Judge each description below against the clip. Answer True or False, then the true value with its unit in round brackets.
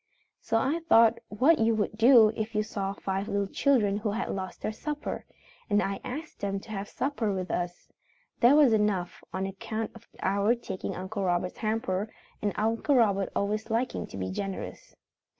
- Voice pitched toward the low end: False (215 Hz)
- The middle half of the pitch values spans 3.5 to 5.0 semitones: False (2.7 semitones)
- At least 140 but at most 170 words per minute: False (180 wpm)